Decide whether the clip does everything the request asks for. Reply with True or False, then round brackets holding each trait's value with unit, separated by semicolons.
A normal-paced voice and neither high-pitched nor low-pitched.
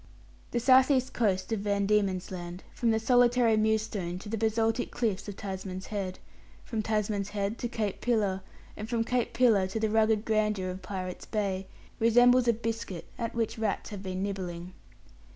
False (175 wpm; 215 Hz)